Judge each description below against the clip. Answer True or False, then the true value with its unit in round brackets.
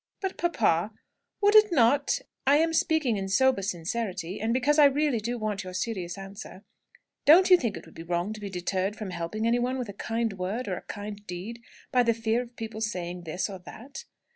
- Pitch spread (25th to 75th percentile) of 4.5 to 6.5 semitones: True (4.8 semitones)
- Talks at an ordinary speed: False (210 wpm)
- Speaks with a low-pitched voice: False (220 Hz)